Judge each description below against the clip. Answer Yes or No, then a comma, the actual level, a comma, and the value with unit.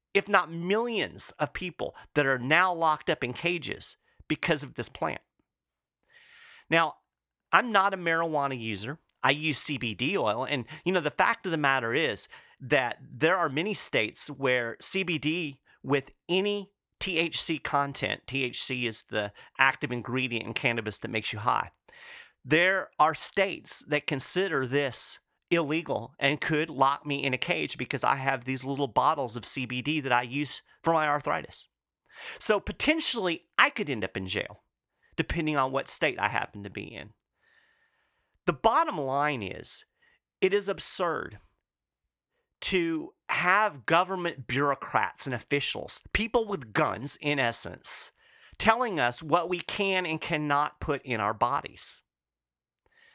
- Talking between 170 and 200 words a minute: No, average, 150 wpm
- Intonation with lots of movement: Yes, wide, 6.0 semitones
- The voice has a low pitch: No, medium, 150 Hz